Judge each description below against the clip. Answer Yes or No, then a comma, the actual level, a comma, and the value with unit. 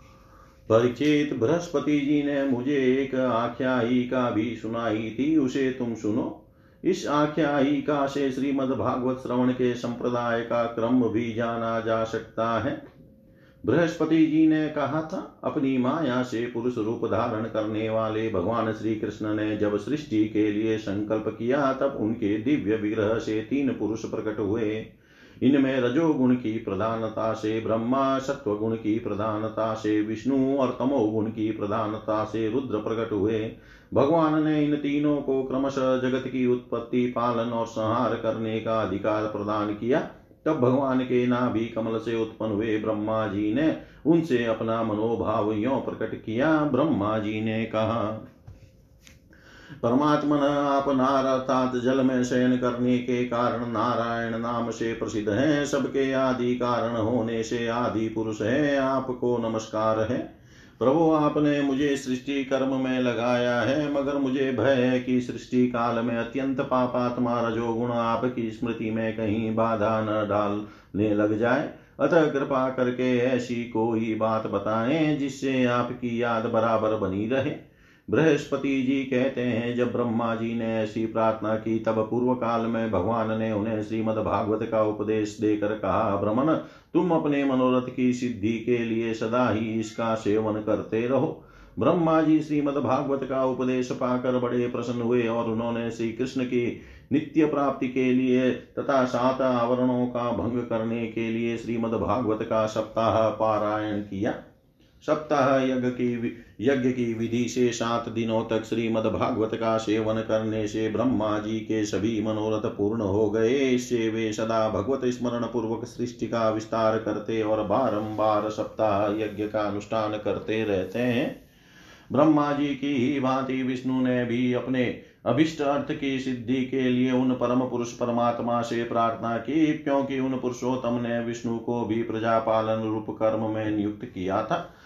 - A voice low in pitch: Yes, low, 115 Hz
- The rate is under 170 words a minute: Yes, average, 150 wpm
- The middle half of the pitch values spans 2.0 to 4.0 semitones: Yes, average, 2.7 semitones